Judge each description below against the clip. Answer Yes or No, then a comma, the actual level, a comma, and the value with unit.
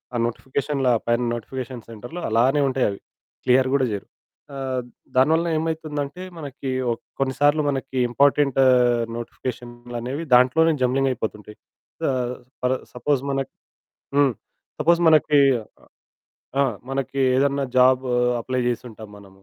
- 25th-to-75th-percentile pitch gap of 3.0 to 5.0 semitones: No, narrow, 2.6 semitones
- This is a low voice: Yes, low, 130 Hz